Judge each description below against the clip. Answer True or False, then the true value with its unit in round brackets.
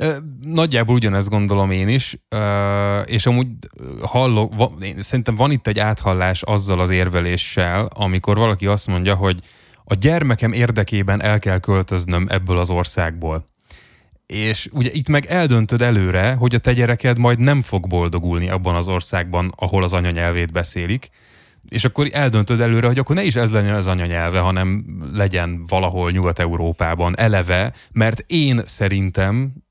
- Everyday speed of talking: True (145 wpm)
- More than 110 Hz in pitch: False (100 Hz)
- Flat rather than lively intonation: False (4.7 semitones)